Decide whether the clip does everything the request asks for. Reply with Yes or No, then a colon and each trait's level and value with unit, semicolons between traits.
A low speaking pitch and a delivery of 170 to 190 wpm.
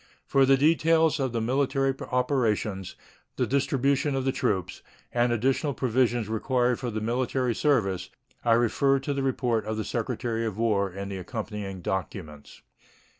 No: low, 120 Hz; average, 155 wpm